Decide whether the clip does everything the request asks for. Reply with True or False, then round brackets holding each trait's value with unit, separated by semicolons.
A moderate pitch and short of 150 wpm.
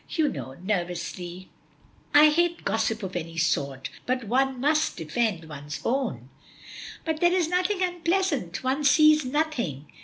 False (250 Hz; 140 wpm)